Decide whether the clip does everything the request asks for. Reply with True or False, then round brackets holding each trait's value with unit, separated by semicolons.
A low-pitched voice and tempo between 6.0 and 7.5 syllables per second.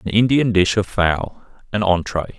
False (100 Hz; 4.4 syllables/s)